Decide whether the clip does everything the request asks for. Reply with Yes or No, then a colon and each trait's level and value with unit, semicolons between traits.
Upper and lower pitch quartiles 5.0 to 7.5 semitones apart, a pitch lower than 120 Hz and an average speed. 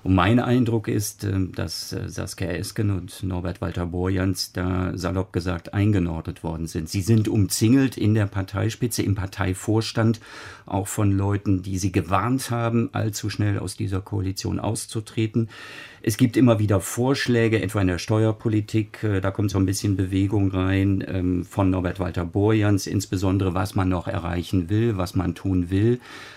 No: average, 2.9 semitones; low, 100 Hz; average, 150 wpm